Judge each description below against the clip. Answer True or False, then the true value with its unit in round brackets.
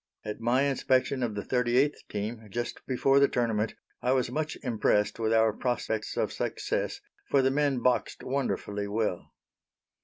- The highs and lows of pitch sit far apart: False (3.4 semitones)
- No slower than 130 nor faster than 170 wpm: True (155 wpm)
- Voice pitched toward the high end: False (120 Hz)